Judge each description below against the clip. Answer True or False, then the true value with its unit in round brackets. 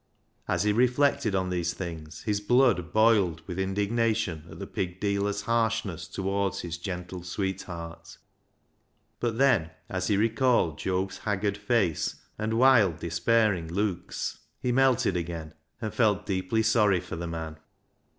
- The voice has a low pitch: True (100 Hz)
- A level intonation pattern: False (4.3 semitones)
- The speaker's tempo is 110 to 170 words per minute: True (140 wpm)